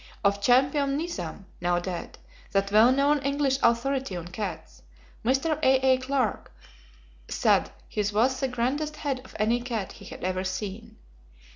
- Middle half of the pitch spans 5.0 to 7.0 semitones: Yes, average, 5.3 semitones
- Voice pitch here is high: Yes, high, 245 Hz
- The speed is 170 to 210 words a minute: No, average, 145 wpm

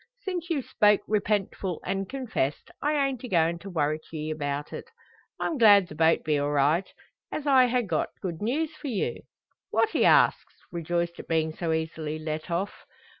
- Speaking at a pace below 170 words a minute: No, average, 180 wpm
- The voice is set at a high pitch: No, medium, 175 Hz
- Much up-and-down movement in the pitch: Yes, wide, 7.9 semitones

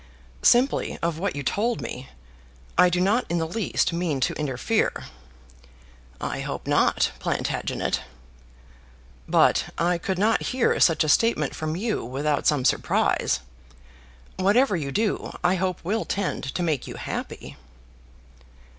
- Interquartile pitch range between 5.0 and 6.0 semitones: Yes, wide, 5.4 semitones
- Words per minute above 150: No, slow, 135 wpm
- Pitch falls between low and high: Yes, medium, 175 Hz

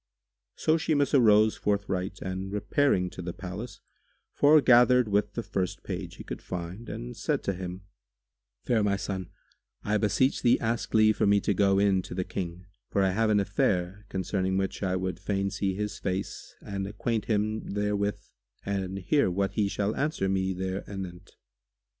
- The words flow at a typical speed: Yes, average, 175 wpm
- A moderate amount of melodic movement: No, narrow, 2.2 semitones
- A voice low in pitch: Yes, low, 100 Hz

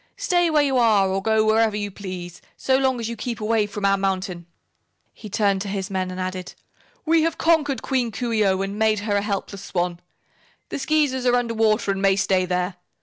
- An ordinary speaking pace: No, fast, 215 wpm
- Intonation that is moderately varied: Yes, average, 4.2 semitones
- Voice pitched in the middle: No, high, 210 Hz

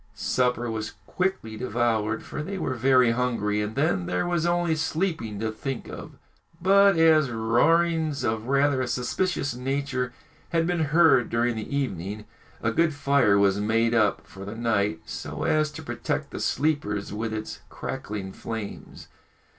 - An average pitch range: No, wide, 6.0 semitones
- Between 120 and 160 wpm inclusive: Yes, average, 155 wpm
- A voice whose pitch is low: Yes, low, 125 Hz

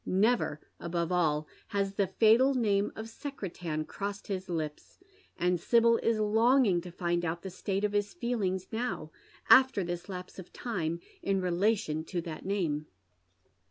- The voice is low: No, high, 190 Hz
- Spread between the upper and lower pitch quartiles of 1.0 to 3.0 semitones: No, average, 4.3 semitones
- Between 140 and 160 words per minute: Yes, average, 155 wpm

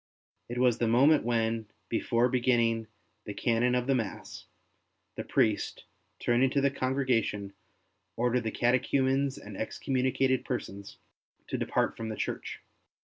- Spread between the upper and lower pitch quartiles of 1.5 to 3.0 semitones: Yes, narrow, 2.5 semitones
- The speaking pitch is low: Yes, low, 120 Hz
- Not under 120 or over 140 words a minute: Yes, slow, 135 wpm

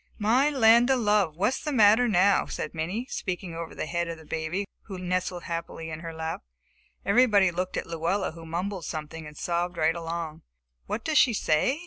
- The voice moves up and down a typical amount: Yes, average, 4.3 semitones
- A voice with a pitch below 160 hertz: No, medium, 180 Hz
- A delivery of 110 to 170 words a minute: No, average, 190 wpm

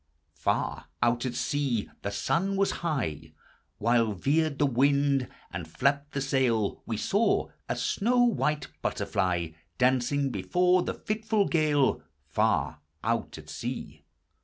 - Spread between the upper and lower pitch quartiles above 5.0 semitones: Yes, wide, 5.4 semitones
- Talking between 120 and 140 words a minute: Yes, slow, 135 wpm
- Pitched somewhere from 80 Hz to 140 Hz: Yes, low, 135 Hz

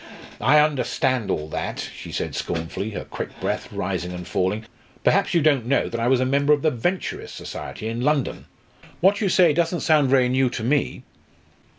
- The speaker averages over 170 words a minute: Yes, average, 190 wpm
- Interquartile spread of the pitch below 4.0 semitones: No, average, 4.8 semitones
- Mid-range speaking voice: No, low, 130 Hz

